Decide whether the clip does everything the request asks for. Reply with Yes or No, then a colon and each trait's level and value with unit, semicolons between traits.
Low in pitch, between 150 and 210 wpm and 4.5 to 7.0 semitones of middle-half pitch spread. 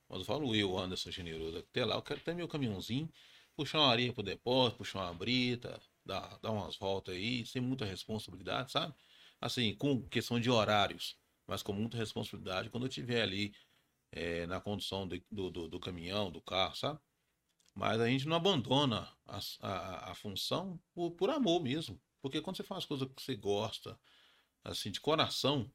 Yes: low, 110 Hz; average, 180 wpm; wide, 5.5 semitones